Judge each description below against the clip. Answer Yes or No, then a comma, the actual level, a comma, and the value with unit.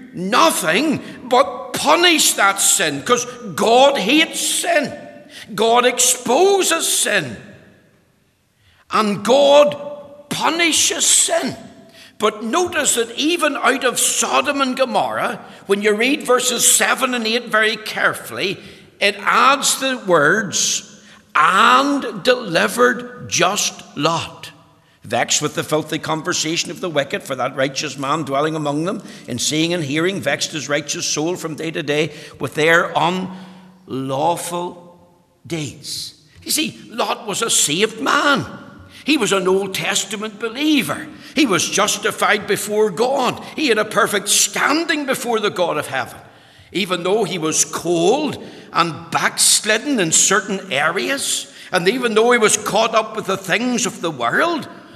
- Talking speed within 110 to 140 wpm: Yes, slow, 135 wpm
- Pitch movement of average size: No, wide, 6.8 semitones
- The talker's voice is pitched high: Yes, high, 205 Hz